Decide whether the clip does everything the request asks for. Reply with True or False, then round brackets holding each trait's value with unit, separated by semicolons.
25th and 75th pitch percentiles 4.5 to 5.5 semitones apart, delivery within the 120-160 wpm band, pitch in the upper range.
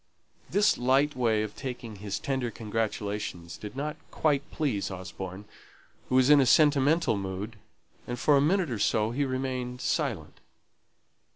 False (5.0 semitones; 150 wpm; 125 Hz)